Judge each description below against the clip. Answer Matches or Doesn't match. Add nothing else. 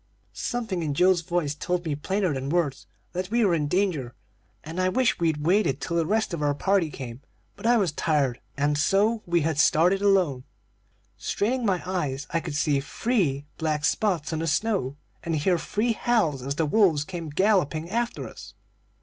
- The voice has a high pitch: Doesn't match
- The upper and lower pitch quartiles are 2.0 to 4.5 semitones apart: Doesn't match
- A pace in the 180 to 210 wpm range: Matches